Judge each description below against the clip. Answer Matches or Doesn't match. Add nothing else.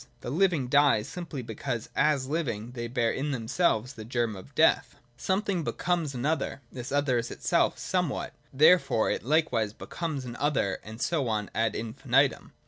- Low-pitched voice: Matches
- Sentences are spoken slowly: Doesn't match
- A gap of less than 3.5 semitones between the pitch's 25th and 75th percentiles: Doesn't match